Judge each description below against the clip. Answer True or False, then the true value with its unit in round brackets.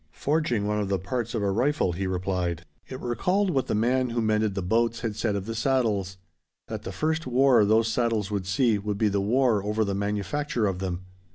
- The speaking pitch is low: True (110 Hz)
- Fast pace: True (215 wpm)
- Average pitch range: True (3.7 semitones)